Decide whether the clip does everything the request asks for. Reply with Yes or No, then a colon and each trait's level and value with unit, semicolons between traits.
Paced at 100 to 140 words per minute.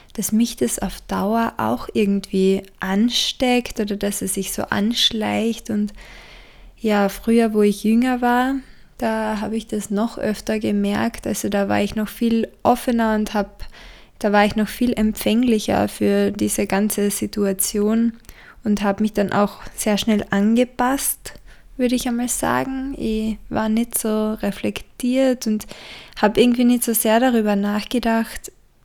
No: average, 150 wpm